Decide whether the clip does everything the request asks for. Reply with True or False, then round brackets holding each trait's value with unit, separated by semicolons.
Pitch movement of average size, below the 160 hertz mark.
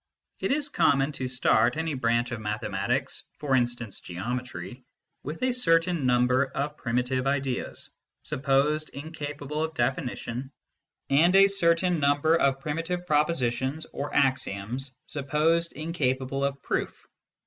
True (4.0 semitones; 140 Hz)